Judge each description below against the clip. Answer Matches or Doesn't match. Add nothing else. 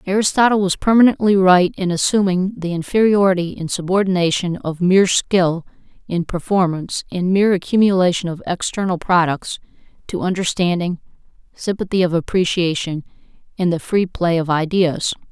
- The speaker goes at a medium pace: Doesn't match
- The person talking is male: Doesn't match